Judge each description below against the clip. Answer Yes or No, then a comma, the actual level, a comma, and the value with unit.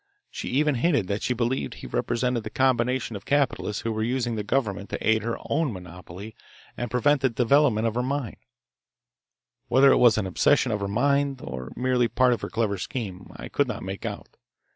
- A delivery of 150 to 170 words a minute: No, average, 200 wpm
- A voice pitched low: Yes, low, 120 Hz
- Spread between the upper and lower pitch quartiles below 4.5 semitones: Yes, average, 3.7 semitones